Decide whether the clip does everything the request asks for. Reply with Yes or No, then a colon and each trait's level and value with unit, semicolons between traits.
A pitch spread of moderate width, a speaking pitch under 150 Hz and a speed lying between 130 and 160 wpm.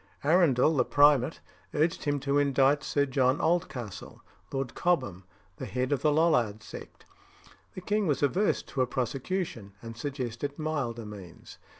Yes: average, 4.2 semitones; medium, 140 Hz; average, 150 wpm